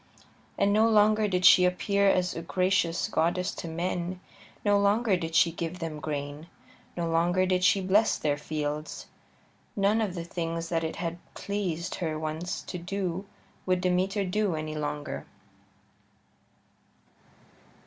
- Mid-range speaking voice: Yes, medium, 180 Hz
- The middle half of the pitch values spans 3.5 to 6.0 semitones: No, average, 3.0 semitones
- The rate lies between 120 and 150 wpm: Yes, average, 145 wpm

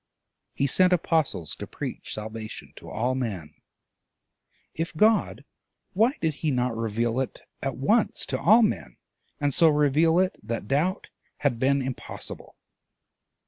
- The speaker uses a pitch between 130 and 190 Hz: Yes, medium, 140 Hz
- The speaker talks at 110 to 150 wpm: Yes, average, 140 wpm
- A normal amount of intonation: No, wide, 6.1 semitones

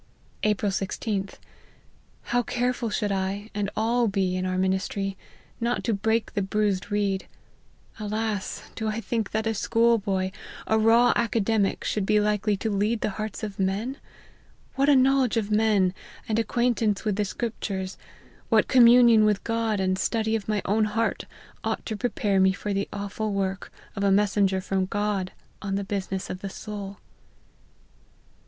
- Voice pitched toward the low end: No, high, 210 Hz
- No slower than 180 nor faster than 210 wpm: No, average, 165 wpm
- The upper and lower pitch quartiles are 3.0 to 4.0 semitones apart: No, narrow, 2.4 semitones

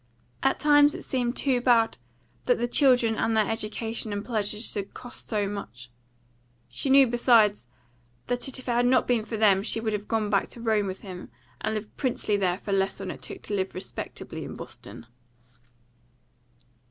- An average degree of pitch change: Yes, average, 3.1 semitones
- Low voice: No, high, 220 Hz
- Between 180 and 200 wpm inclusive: Yes, average, 185 wpm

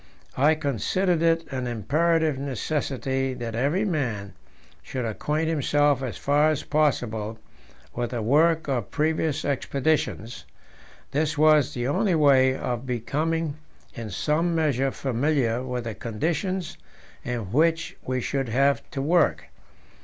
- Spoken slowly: Yes, slow, 130 wpm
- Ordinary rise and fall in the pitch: Yes, average, 4.2 semitones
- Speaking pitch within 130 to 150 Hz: Yes, medium, 140 Hz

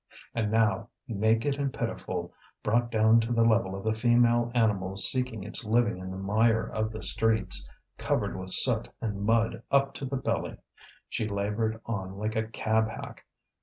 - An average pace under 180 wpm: Yes, average, 170 wpm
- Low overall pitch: Yes, low, 110 Hz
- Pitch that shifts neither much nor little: No, narrow, 1.9 semitones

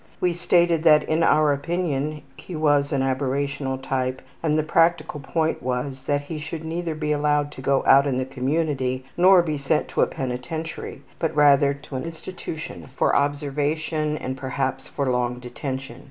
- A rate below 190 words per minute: Yes, average, 170 wpm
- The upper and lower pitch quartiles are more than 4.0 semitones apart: No, average, 3.0 semitones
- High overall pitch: No, medium, 145 Hz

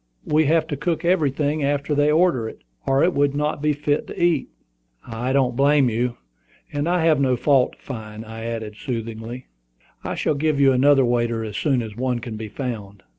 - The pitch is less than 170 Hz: Yes, low, 135 Hz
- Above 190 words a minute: Yes, average, 200 wpm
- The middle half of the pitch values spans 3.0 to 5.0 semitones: Yes, average, 4.1 semitones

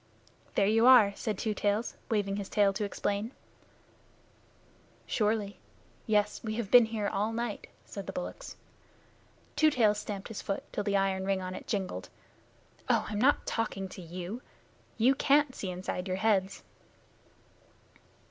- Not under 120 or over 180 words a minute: Yes, average, 150 wpm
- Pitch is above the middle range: Yes, high, 210 Hz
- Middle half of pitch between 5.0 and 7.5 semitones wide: No, narrow, 2.5 semitones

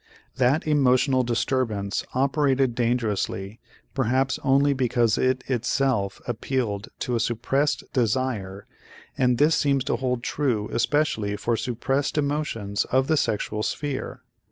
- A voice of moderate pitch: No, low, 125 Hz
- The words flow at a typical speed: No, slow, 120 wpm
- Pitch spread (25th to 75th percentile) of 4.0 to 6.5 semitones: No, average, 3.2 semitones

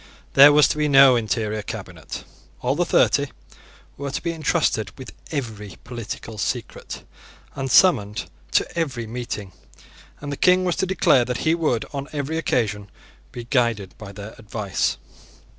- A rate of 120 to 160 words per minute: Yes, average, 155 wpm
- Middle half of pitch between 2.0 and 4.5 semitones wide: No, average, 5.2 semitones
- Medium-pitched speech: No, low, 125 Hz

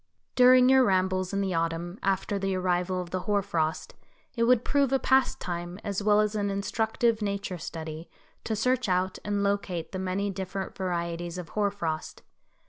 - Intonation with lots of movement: No, average, 2.7 semitones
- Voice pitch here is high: Yes, high, 195 Hz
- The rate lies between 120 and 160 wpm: No, average, 175 wpm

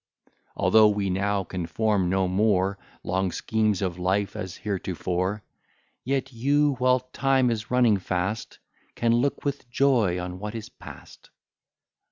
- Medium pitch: No, low, 105 Hz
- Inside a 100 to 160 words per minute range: Yes, average, 140 wpm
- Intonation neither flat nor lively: Yes, average, 4.5 semitones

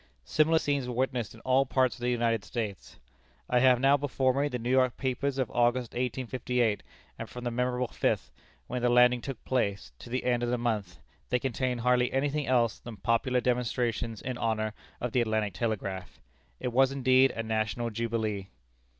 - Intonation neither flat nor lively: No, narrow, 1.9 semitones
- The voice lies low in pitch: Yes, low, 125 Hz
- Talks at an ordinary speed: Yes, average, 190 wpm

